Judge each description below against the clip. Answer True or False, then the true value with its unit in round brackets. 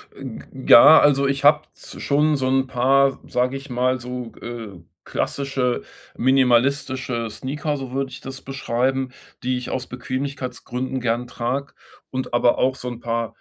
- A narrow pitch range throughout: True (1.8 semitones)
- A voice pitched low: True (130 Hz)